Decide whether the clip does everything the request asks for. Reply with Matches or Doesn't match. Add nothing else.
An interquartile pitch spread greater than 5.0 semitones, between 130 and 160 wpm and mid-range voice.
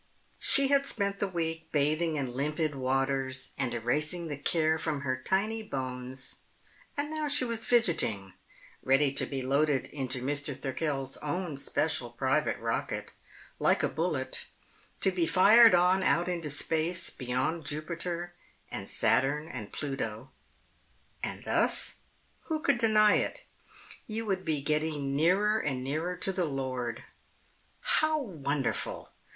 Matches